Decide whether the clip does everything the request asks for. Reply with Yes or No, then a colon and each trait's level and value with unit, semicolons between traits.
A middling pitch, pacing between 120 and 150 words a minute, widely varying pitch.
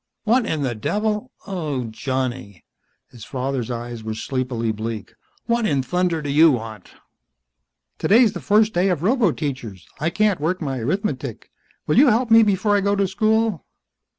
No: medium, 155 Hz; average, 160 wpm; wide, 9.0 semitones